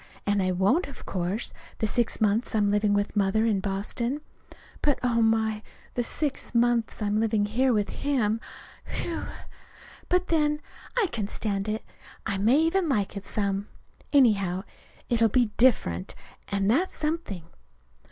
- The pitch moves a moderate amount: Yes, average, 4.0 semitones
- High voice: Yes, high, 220 Hz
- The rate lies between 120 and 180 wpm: Yes, average, 150 wpm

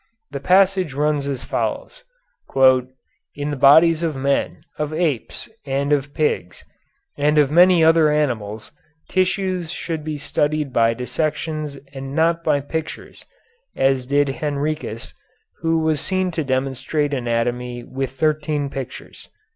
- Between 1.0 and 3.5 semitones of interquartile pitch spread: Yes, average, 2.9 semitones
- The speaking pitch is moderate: Yes, medium, 145 Hz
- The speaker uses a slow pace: Yes, slow, 130 wpm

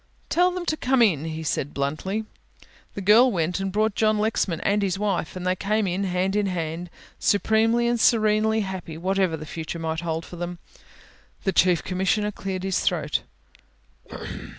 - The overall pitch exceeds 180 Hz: Yes, high, 190 Hz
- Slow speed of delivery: No, average, 175 wpm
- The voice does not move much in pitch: No, average, 3.7 semitones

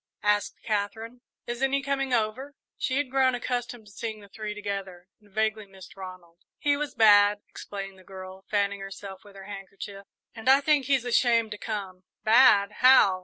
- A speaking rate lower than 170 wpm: No, average, 175 wpm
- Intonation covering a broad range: No, average, 3.9 semitones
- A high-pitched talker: Yes, high, 210 Hz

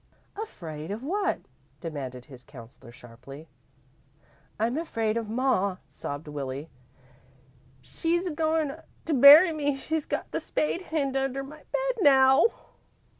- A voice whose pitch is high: Yes, very high, 265 Hz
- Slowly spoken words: Yes, slow, 125 wpm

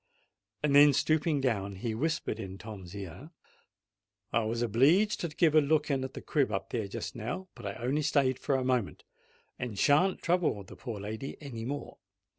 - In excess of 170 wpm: Yes, average, 180 wpm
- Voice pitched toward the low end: Yes, low, 130 Hz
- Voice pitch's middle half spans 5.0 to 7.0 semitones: Yes, wide, 5.5 semitones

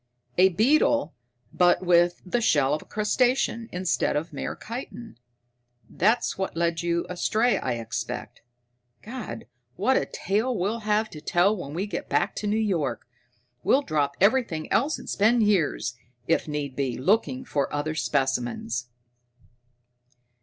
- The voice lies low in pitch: No, medium, 180 Hz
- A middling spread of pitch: No, wide, 7.0 semitones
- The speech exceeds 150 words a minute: No, average, 145 wpm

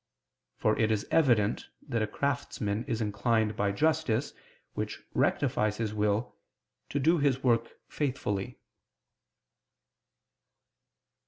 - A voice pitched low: Yes, low, 115 Hz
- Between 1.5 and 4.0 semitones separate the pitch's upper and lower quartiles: No, average, 4.4 semitones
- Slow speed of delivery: Yes, slow, 105 wpm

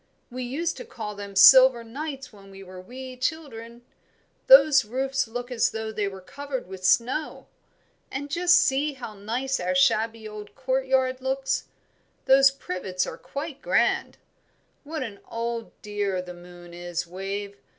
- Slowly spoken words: No, average, 150 wpm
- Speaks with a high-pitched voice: Yes, high, 240 Hz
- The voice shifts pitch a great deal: No, average, 5.0 semitones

